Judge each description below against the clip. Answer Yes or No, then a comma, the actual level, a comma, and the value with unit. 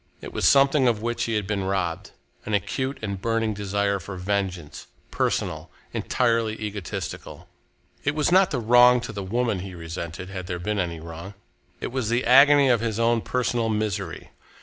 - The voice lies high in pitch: No, low, 105 Hz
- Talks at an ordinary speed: Yes, average, 180 wpm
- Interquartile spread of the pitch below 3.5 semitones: No, average, 4.1 semitones